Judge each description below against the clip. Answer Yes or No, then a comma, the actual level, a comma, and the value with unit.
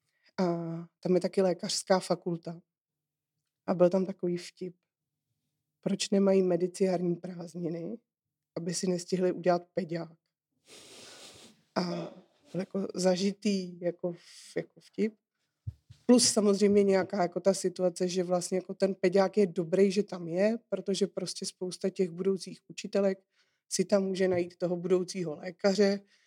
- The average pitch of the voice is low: No, medium, 185 Hz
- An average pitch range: No, narrow, 2.0 semitones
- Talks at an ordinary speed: Yes, average, 130 wpm